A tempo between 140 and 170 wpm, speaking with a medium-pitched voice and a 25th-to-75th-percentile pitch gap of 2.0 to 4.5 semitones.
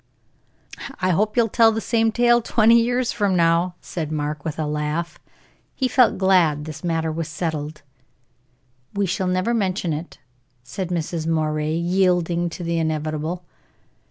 Yes: average, 150 wpm; medium, 170 Hz; average, 4.0 semitones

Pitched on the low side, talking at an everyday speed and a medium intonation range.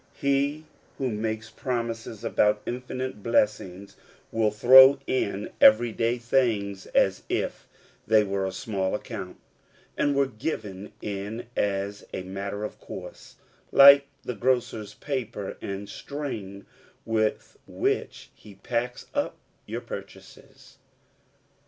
No: low, 110 Hz; slow, 115 wpm; average, 4.2 semitones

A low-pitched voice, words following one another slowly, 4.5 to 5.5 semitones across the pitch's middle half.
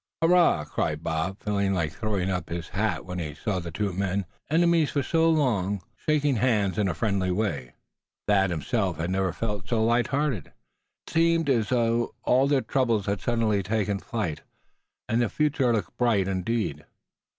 No: low, 105 Hz; average, 175 wpm; average, 4.9 semitones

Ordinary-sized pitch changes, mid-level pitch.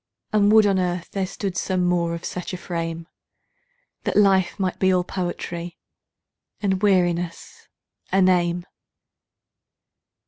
No: narrow, 1.9 semitones; medium, 180 Hz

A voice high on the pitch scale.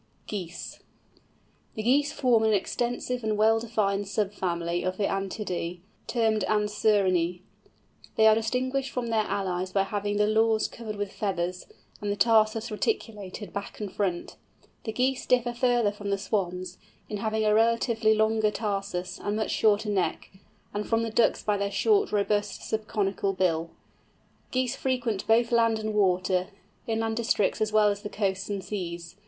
Yes: high, 210 Hz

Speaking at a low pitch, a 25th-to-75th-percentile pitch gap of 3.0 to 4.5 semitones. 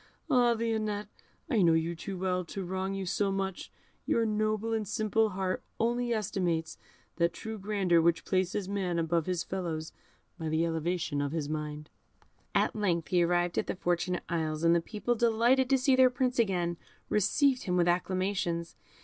No: medium, 185 Hz; average, 4.2 semitones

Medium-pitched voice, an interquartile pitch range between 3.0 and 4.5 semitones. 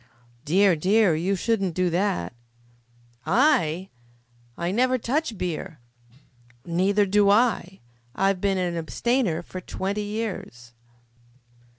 No: high, 195 Hz; average, 3.6 semitones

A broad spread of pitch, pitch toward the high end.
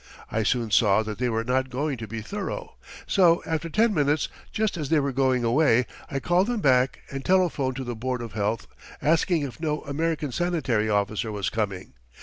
No: wide, 5.9 semitones; low, 130 Hz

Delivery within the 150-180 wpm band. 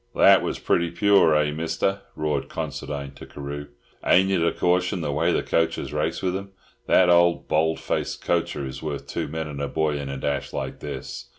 No: average, 200 wpm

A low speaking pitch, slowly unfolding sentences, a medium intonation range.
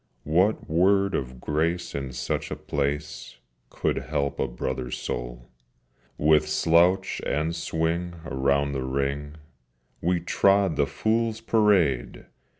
Yes: very low, 75 Hz; slow, 120 wpm; average, 4.3 semitones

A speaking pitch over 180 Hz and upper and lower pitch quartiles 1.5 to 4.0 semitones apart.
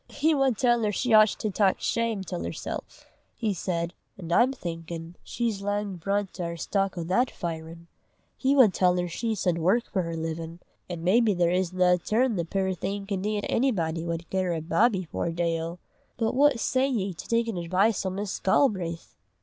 No: high, 190 Hz; average, 4.7 semitones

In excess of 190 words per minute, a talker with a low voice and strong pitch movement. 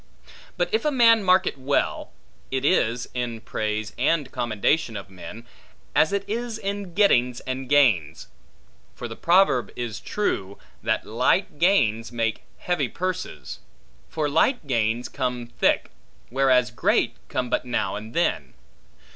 No: average, 140 wpm; low, 130 Hz; wide, 7.8 semitones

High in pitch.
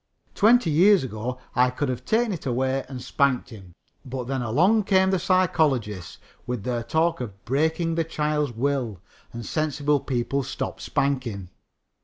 No: low, 135 Hz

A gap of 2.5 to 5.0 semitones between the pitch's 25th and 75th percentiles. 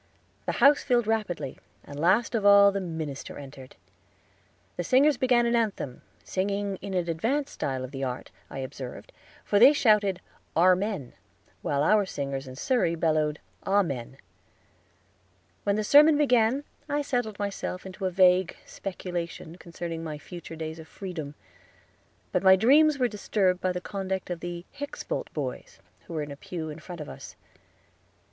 No: wide, 5.5 semitones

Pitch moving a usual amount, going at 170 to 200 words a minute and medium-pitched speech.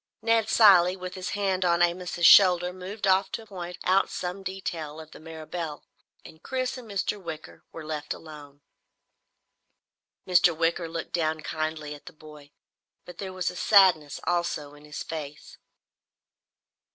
No: average, 3.2 semitones; average, 150 wpm; medium, 175 Hz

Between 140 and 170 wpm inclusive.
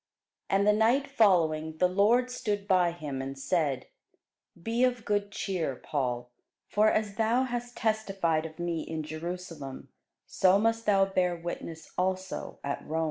Yes: average, 150 wpm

